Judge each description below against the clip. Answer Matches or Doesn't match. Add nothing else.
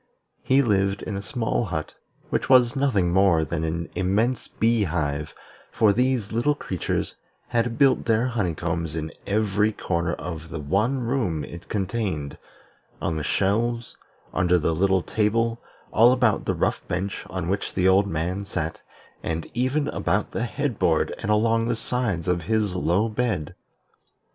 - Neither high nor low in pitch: Doesn't match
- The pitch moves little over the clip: Doesn't match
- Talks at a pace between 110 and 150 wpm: Doesn't match